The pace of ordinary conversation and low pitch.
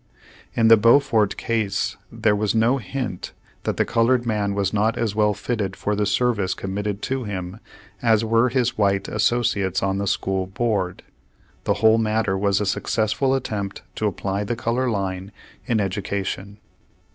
Yes: average, 160 wpm; low, 105 Hz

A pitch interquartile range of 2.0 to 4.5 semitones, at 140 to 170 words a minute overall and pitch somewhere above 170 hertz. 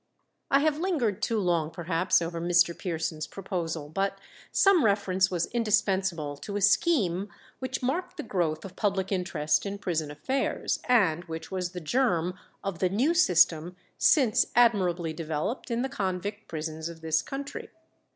No: average, 5.3 semitones; average, 155 wpm; medium, 185 Hz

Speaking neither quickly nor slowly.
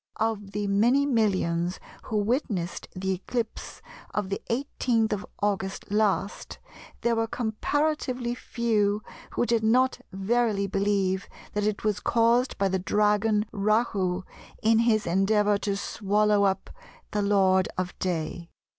No: slow, 130 wpm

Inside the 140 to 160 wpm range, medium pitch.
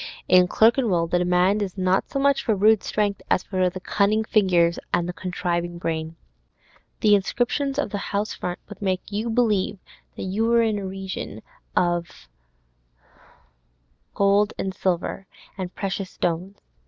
No: average, 155 wpm; high, 195 Hz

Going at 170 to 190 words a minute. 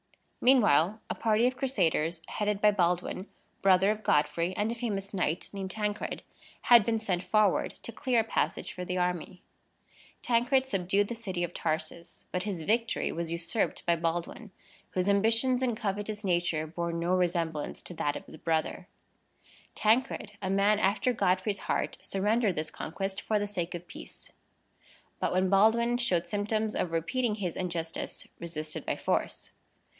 No: average, 160 wpm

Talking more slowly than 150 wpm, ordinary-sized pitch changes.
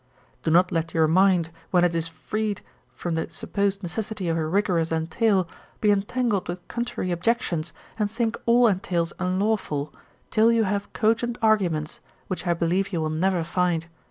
No: average, 165 wpm; average, 4.2 semitones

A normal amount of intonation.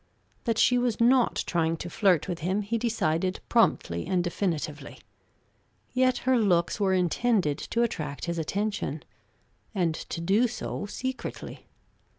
No: wide, 5.7 semitones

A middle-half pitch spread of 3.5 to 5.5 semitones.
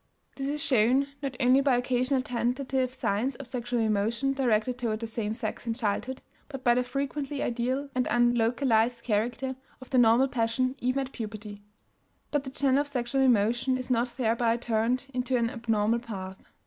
No: narrow, 2.5 semitones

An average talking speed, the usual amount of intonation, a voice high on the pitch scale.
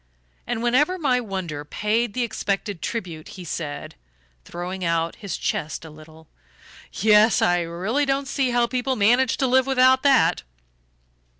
No: average, 145 wpm; wide, 6.8 semitones; high, 215 Hz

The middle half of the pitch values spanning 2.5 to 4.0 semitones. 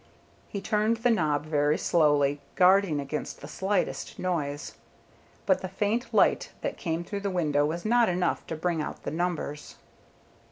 No: average, 4.8 semitones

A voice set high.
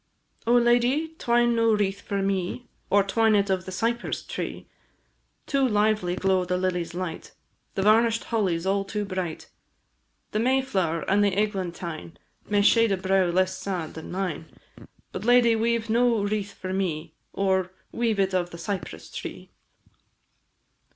Yes: high, 195 Hz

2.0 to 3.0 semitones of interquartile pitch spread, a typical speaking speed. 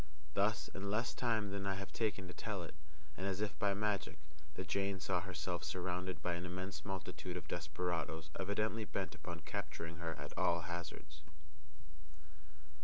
Yes: narrow, 2.5 semitones; average, 165 wpm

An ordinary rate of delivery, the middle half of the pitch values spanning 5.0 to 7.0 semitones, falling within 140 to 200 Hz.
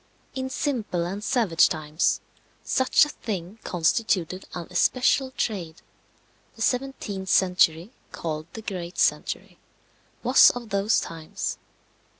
No: slow, 115 wpm; wide, 5.5 semitones; high, 190 Hz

